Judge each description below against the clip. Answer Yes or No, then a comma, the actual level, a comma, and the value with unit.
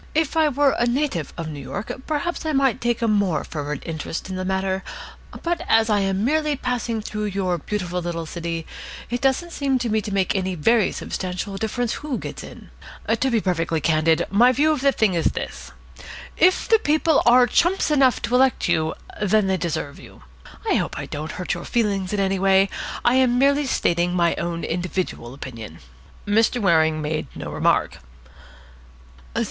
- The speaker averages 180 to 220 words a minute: Yes, average, 185 wpm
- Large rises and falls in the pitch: Yes, wide, 6.7 semitones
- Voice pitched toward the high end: Yes, high, 200 Hz